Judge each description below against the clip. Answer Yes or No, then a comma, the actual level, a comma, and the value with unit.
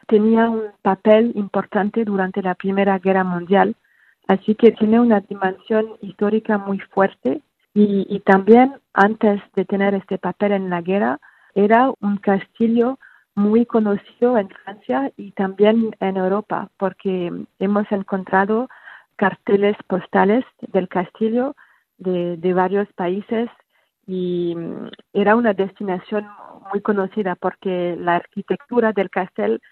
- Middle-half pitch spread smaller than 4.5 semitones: Yes, narrow, 2.4 semitones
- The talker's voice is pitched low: No, high, 200 Hz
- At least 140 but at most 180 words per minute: No, slow, 125 wpm